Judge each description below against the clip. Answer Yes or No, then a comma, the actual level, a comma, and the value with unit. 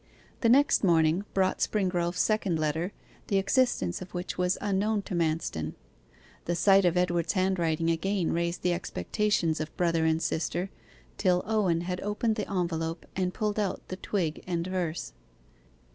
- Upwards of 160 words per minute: No, average, 155 wpm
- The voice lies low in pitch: No, medium, 180 Hz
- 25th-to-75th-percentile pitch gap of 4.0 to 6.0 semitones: No, average, 2.9 semitones